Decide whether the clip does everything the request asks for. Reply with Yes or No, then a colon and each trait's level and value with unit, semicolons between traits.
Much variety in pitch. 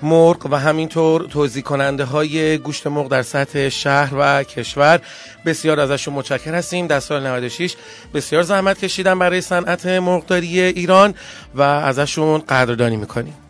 No: average, 3.9 semitones